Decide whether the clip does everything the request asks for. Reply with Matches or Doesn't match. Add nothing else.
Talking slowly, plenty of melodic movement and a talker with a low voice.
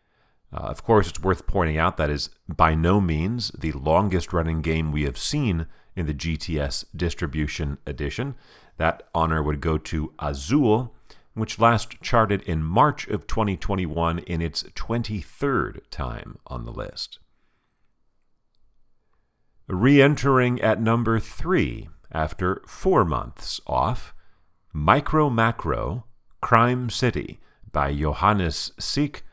Matches